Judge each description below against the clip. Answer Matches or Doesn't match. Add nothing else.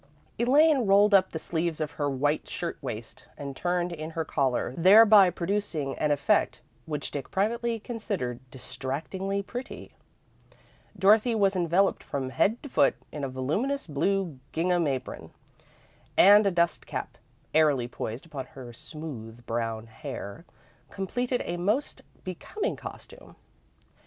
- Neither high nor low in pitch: Matches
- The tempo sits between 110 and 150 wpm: Matches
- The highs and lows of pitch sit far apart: Matches